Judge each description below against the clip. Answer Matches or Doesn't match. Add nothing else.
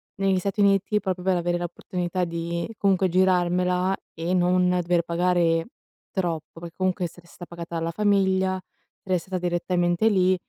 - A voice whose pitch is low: Doesn't match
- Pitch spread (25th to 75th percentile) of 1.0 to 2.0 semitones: Matches